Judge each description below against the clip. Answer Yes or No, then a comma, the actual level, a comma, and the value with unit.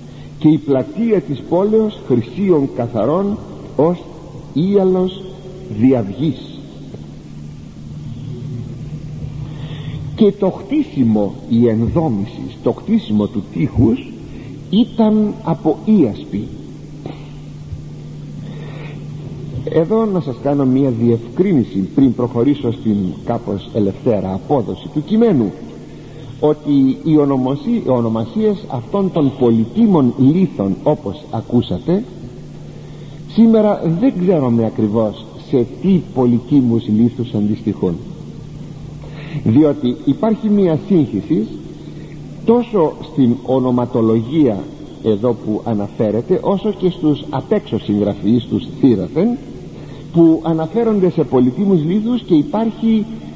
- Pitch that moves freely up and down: Yes, wide, 6.4 semitones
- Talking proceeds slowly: Yes, slow, 90 wpm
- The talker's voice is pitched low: No, medium, 145 Hz